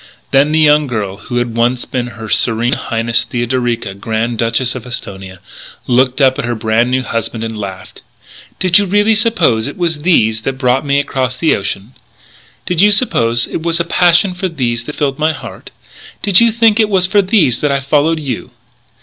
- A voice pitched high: No, low, 130 Hz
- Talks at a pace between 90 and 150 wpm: No, average, 195 wpm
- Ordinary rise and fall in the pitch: No, wide, 6.2 semitones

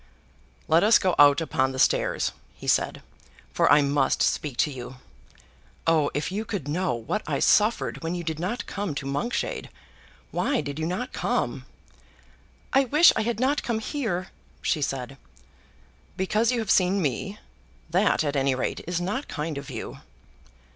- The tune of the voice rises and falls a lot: Yes, wide, 6.7 semitones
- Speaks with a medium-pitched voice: Yes, medium, 170 Hz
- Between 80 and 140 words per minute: No, average, 170 wpm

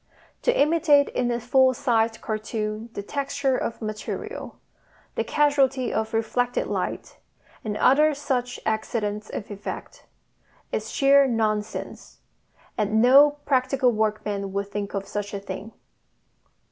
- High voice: Yes, high, 230 Hz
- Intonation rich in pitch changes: No, average, 4.1 semitones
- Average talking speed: No, slow, 125 wpm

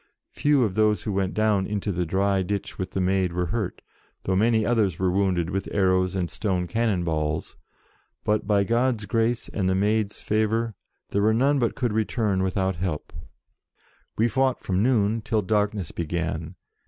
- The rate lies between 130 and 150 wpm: No, average, 175 wpm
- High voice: No, low, 100 Hz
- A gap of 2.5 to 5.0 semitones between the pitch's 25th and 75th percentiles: Yes, average, 3.0 semitones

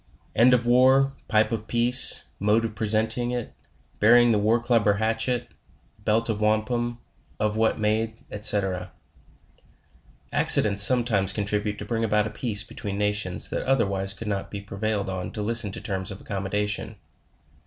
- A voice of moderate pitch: No, low, 110 Hz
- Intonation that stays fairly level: Yes, narrow, 2.2 semitones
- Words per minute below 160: No, average, 165 wpm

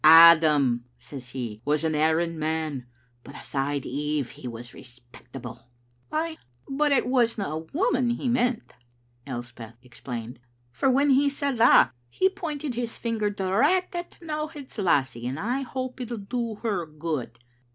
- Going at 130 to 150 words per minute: No, average, 160 wpm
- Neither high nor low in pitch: Yes, medium, 165 Hz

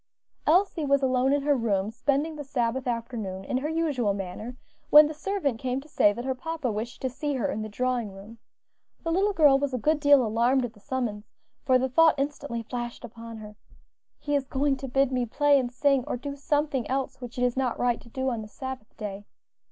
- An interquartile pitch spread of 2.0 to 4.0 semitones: Yes, average, 3.6 semitones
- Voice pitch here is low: No, very high, 260 Hz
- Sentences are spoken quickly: Yes, fast, 225 wpm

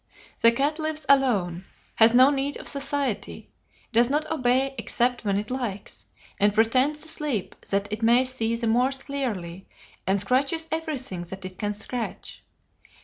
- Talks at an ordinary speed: Yes, average, 155 wpm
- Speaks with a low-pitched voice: No, high, 245 Hz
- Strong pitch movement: No, average, 4.9 semitones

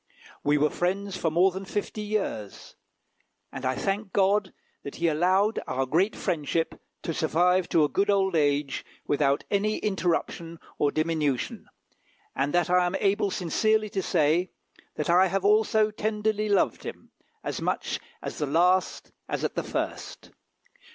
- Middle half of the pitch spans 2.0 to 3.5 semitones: No, average, 4.4 semitones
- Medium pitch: Yes, medium, 180 Hz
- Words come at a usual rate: Yes, average, 155 wpm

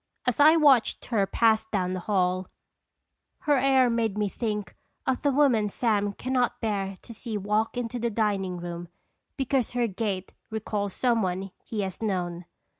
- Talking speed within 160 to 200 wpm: Yes, average, 170 wpm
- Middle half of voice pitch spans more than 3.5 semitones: Yes, average, 3.9 semitones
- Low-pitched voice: No, high, 215 Hz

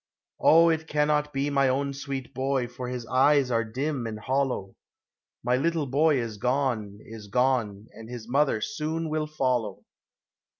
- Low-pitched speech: Yes, low, 130 Hz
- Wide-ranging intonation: No, average, 3.9 semitones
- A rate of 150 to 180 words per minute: Yes, average, 165 wpm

